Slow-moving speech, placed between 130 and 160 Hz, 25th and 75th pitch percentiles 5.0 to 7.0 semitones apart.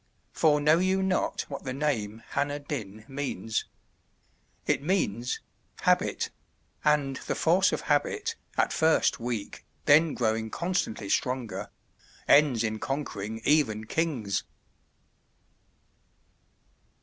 Yes: slow, 105 wpm; medium, 140 Hz; wide, 5.6 semitones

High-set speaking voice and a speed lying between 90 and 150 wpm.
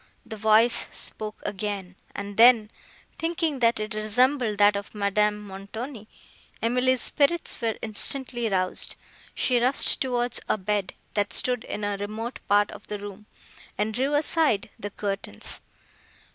Yes: high, 215 Hz; average, 140 wpm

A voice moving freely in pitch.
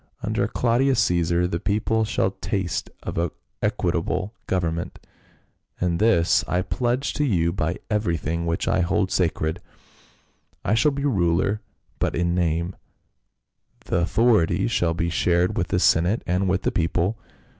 No: average, 4.1 semitones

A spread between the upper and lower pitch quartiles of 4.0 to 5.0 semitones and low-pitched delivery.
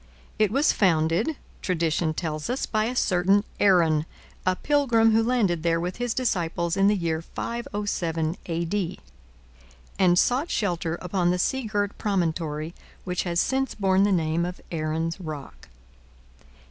No: average, 4.3 semitones; medium, 180 Hz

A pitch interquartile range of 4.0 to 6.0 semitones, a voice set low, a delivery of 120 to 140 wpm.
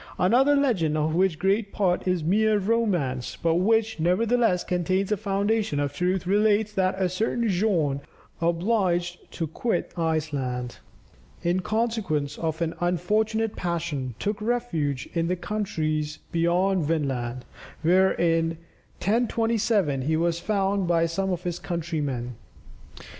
No: average, 4.6 semitones; medium, 180 Hz; slow, 135 wpm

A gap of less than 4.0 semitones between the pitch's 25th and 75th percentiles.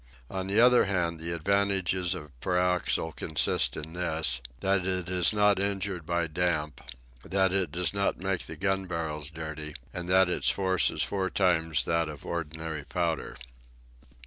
Yes: average, 2.9 semitones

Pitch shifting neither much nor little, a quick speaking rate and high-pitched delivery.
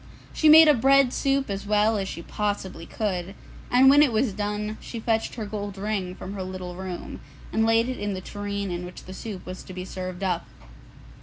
Yes: average, 3.3 semitones; fast, 215 wpm; high, 205 Hz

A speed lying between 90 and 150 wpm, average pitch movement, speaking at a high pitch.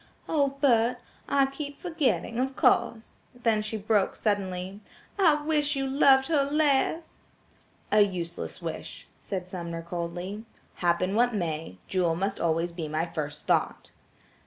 No: slow, 135 wpm; wide, 7.8 semitones; high, 210 Hz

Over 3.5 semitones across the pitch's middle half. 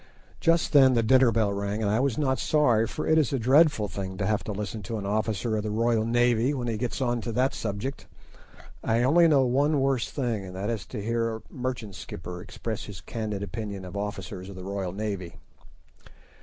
Yes: average, 4.1 semitones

